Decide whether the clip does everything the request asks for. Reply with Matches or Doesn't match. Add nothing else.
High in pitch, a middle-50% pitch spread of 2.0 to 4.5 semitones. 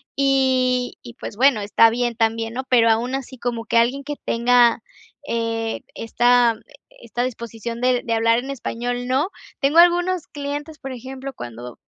Matches